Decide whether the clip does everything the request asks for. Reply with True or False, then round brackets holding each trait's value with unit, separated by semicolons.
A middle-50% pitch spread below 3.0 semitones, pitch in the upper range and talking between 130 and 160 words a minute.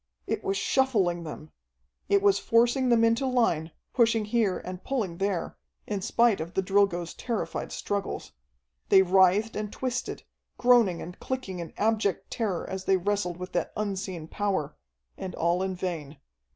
False (4.0 semitones; 195 Hz; 155 wpm)